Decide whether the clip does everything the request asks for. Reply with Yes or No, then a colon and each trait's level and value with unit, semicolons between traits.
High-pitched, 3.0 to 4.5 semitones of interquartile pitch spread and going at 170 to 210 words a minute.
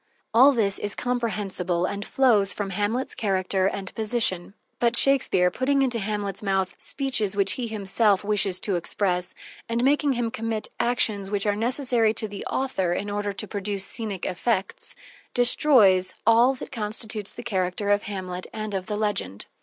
No: high, 210 Hz; average, 3.3 semitones; average, 160 wpm